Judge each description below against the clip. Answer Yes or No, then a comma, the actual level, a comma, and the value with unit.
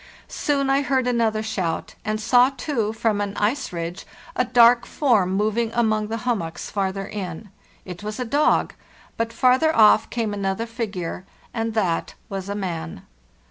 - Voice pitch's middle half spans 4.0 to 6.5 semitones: No, average, 3.6 semitones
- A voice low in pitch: No, high, 220 Hz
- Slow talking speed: No, average, 155 wpm